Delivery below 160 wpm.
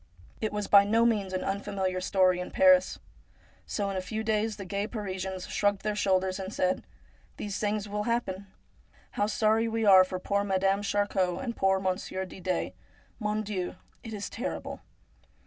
No: average, 180 wpm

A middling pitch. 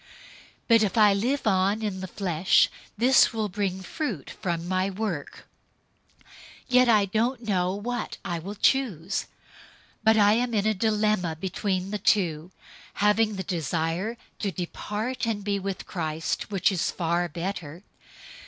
No: high, 200 Hz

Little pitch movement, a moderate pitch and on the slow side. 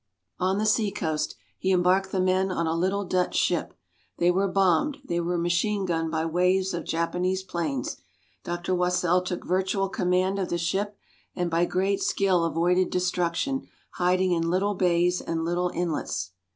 No: narrow, 1.8 semitones; medium, 180 Hz; average, 165 wpm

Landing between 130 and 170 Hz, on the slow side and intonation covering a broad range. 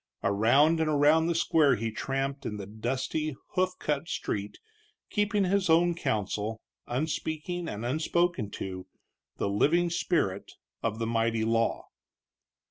Yes: medium, 140 Hz; slow, 130 wpm; wide, 6.9 semitones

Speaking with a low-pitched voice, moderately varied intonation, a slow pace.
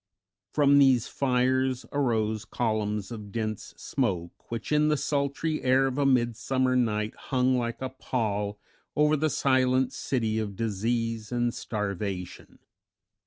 Yes: low, 120 Hz; average, 3.5 semitones; slow, 130 wpm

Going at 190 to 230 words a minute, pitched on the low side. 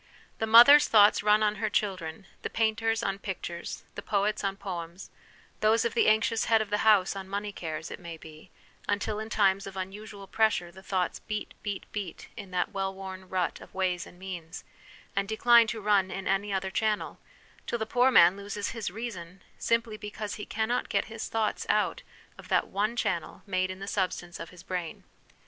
No: average, 200 wpm; high, 200 Hz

